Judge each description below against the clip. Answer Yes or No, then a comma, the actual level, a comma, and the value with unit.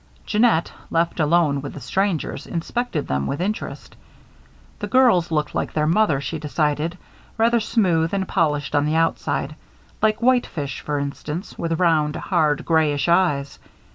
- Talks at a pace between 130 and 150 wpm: Yes, average, 145 wpm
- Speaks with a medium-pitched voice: Yes, medium, 165 Hz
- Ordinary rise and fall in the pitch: Yes, average, 4.3 semitones